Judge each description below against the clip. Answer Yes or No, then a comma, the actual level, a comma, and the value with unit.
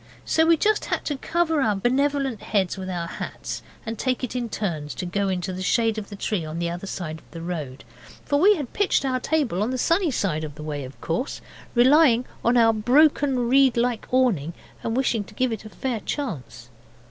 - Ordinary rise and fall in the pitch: No, wide, 6.9 semitones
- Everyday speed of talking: No, fast, 215 wpm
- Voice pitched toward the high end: Yes, high, 225 Hz